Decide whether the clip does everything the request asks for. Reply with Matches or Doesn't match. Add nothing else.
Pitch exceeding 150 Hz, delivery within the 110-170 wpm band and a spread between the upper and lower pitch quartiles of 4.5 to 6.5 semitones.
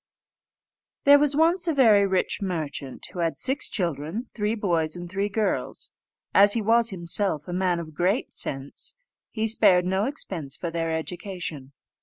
Matches